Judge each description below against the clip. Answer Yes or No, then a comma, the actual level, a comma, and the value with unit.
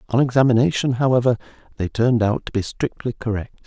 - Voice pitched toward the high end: No, low, 120 Hz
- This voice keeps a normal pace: Yes, average, 165 wpm